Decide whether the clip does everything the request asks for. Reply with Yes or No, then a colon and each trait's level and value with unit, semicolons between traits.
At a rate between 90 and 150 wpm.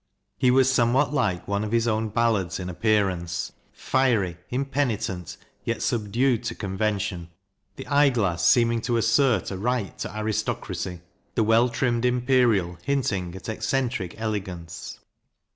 Yes: average, 145 wpm